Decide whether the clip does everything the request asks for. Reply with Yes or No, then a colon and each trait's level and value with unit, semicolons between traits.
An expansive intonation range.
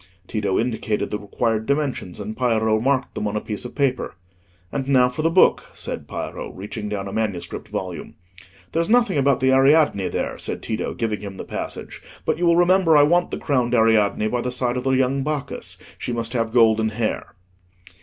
No: average, 4.4 semitones